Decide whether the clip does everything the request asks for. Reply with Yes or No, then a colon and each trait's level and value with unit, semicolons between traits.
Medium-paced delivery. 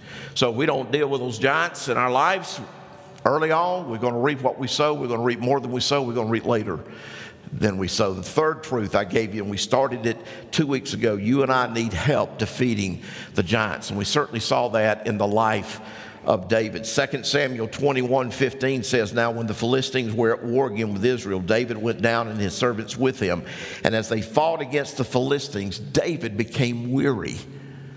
No: fast, 215 wpm